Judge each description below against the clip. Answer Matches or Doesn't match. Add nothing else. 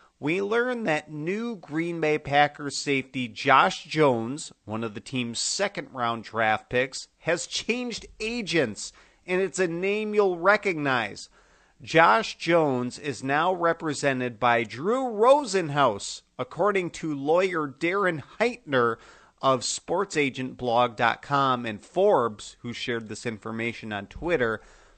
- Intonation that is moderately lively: Doesn't match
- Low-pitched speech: Doesn't match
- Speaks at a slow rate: Matches